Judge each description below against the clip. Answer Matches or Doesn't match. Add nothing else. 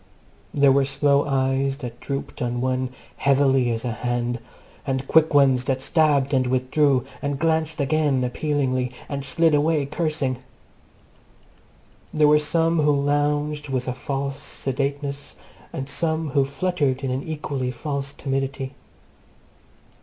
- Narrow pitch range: Matches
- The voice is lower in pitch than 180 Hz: Matches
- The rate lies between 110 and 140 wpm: Matches